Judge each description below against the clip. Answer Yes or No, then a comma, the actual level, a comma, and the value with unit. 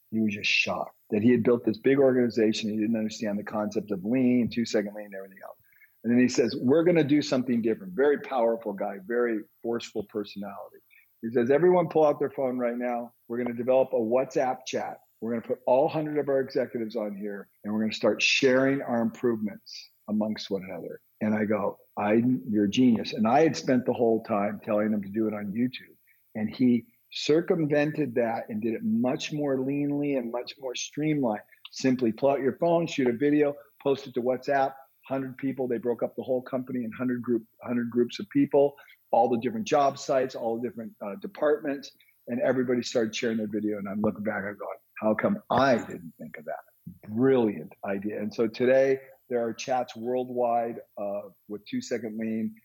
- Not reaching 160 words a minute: No, fast, 205 wpm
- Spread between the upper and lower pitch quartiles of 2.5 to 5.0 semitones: Yes, average, 3.7 semitones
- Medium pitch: No, low, 120 Hz